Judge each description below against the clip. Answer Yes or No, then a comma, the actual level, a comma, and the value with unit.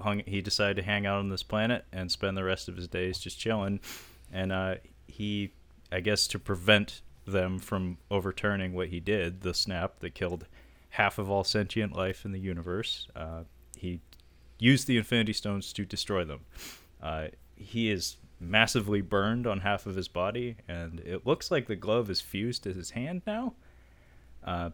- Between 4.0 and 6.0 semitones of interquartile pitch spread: No, average, 3.2 semitones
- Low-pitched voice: Yes, very low, 95 Hz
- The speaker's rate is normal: Yes, average, 180 wpm